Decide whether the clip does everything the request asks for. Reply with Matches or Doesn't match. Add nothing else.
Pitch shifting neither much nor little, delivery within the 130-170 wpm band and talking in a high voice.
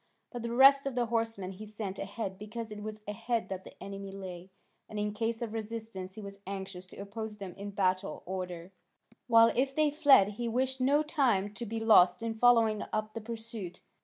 Doesn't match